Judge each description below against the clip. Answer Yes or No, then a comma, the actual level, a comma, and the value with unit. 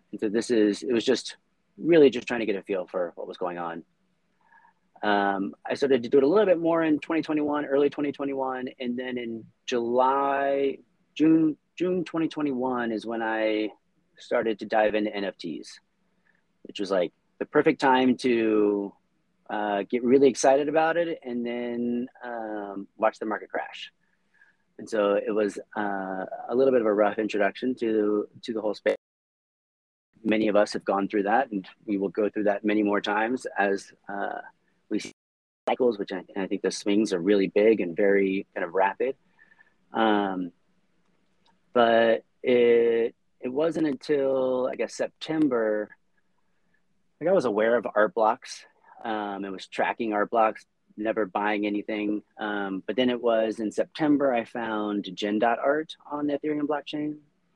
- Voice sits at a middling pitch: No, low, 115 Hz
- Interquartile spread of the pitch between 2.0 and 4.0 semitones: No, average, 4.7 semitones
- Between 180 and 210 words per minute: No, average, 165 wpm